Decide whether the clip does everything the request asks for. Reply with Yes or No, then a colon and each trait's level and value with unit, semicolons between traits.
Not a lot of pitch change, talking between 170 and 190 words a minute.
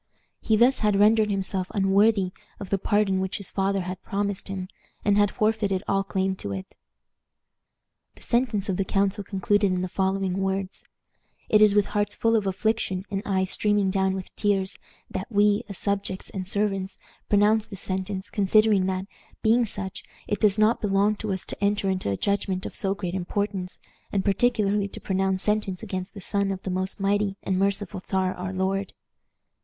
Yes: narrow, 1.5 semitones; average, 180 wpm